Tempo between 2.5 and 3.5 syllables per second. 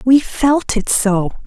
Yes: 3.2 syllables/s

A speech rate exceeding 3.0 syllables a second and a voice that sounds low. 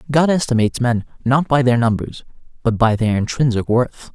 Yes: 5.4 syllables/s; low, 125 Hz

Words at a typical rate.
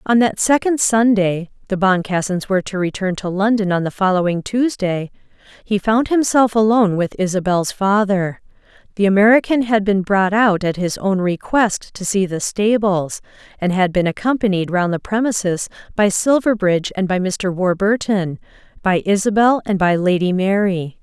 Yes: average, 150 wpm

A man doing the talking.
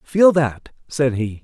Yes: male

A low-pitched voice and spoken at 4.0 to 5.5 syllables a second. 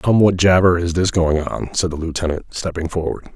Yes: very low, 85 Hz; 5.3 syllables/s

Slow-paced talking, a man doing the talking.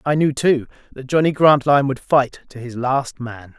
No: average, 200 wpm; male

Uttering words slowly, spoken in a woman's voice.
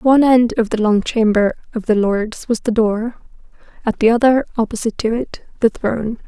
No: average, 200 wpm; female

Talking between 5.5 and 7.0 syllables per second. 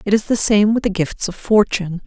Yes: 5.7 syllables/s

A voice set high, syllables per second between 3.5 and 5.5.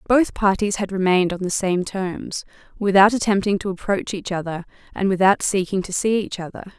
Yes: high, 195 Hz; 5.4 syllables/s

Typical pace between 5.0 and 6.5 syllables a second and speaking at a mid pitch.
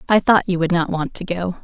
Yes: 5.7 syllables/s; medium, 180 Hz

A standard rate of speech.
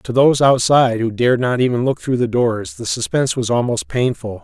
No: fast, 215 wpm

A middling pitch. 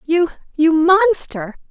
No: very high, 325 Hz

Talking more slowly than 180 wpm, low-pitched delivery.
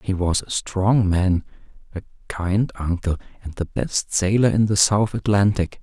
Yes: average, 165 wpm; very low, 95 Hz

